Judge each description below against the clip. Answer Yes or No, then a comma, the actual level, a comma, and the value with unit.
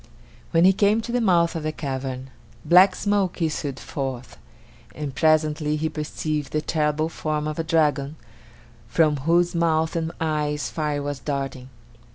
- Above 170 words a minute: No, average, 155 wpm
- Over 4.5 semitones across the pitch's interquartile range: No, narrow, 2.4 semitones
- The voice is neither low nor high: Yes, medium, 155 Hz